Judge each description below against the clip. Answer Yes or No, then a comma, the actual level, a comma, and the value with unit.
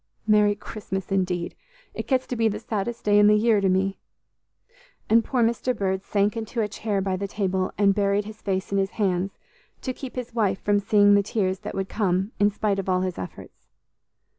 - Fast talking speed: Yes, fast, 210 wpm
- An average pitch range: No, narrow, 2.1 semitones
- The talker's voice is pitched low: No, high, 205 Hz